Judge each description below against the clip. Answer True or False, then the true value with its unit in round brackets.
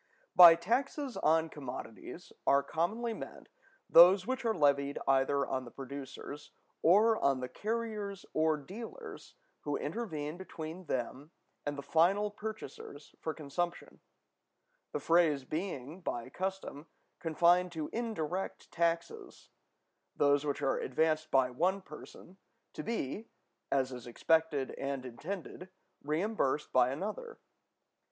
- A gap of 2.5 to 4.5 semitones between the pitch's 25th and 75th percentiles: False (5.5 semitones)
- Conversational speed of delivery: False (120 wpm)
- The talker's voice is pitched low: False (160 Hz)